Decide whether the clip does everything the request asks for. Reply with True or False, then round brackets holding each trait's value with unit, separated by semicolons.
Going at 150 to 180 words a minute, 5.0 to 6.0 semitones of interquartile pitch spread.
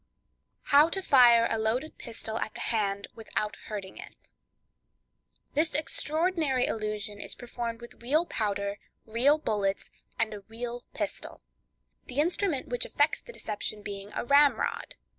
False (135 wpm; 5.3 semitones)